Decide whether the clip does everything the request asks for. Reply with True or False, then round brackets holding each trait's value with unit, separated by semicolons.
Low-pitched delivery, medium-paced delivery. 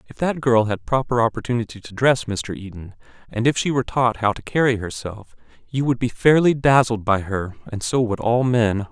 False (115 Hz; 210 wpm)